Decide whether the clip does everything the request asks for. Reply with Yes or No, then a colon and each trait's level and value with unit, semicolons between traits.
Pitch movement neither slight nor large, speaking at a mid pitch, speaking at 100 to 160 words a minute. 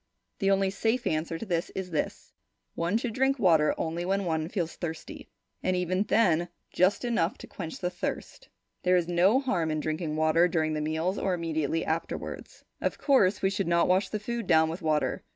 No: average, 3.4 semitones; medium, 175 Hz; average, 200 wpm